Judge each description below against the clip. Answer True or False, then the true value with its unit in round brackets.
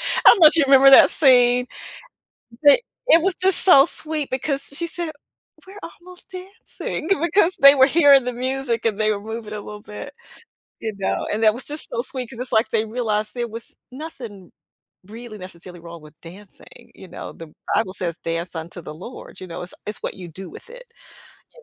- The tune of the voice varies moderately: False (6.3 semitones)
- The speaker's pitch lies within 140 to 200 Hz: False (240 Hz)